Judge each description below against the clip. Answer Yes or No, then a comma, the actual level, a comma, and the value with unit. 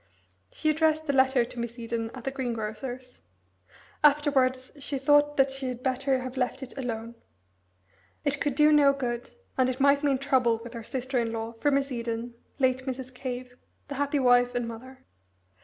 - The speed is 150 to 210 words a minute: Yes, average, 180 wpm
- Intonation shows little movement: Yes, narrow, 2.3 semitones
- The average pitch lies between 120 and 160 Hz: No, very high, 260 Hz